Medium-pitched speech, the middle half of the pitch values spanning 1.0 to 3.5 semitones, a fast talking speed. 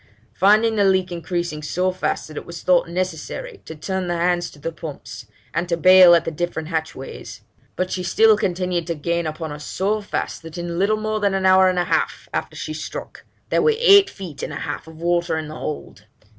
Yes: medium, 175 Hz; narrow, 2.6 semitones; fast, 215 wpm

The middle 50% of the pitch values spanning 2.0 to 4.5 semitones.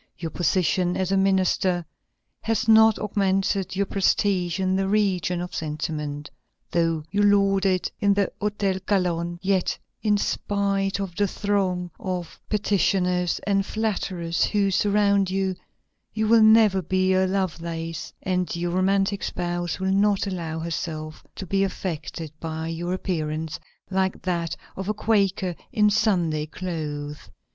Yes: narrow, 2.6 semitones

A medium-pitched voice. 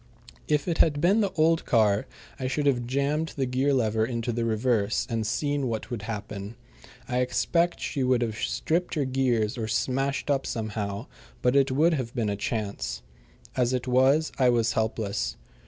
No: low, 125 Hz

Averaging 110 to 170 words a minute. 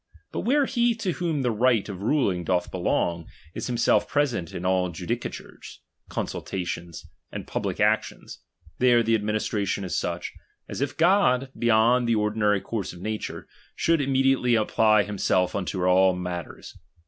Yes: average, 150 wpm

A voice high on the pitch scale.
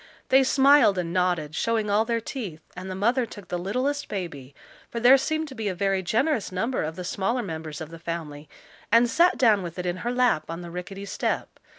Yes: high, 195 Hz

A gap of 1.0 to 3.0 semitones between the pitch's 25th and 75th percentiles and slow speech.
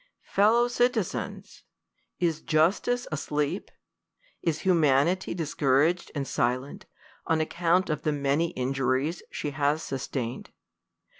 No: average, 3.8 semitones; slow, 105 wpm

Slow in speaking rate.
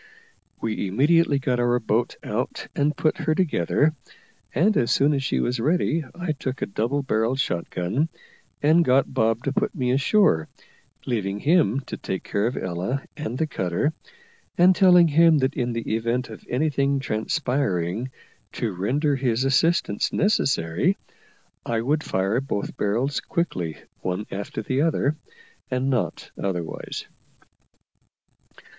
No: average, 145 wpm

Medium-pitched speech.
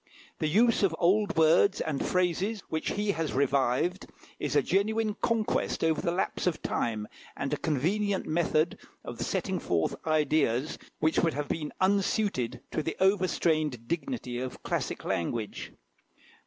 Yes: medium, 165 Hz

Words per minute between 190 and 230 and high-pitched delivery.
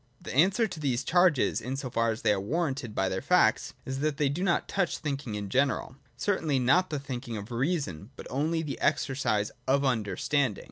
No: average, 200 wpm; low, 135 Hz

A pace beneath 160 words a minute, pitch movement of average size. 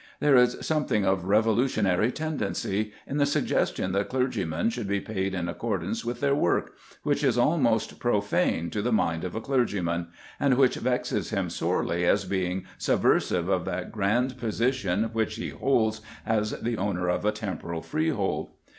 No: average, 165 wpm; average, 4.7 semitones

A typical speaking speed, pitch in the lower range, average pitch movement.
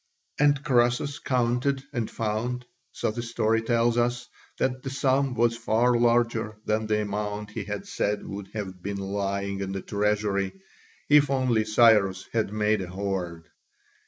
Yes: average, 155 wpm; low, 110 Hz; average, 3.2 semitones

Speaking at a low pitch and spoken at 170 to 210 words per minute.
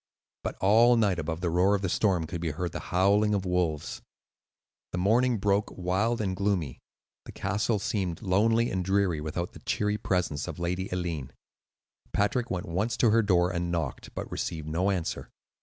Yes: very low, 95 Hz; average, 180 wpm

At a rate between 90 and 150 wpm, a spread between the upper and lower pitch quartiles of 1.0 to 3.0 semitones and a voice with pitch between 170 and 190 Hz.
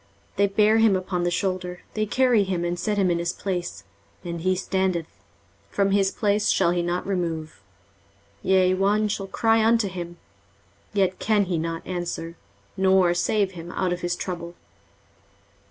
No: average, 170 wpm; narrow, 2.5 semitones; medium, 185 Hz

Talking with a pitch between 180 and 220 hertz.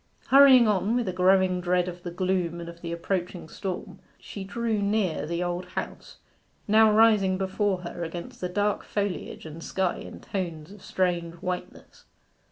Yes: medium, 185 Hz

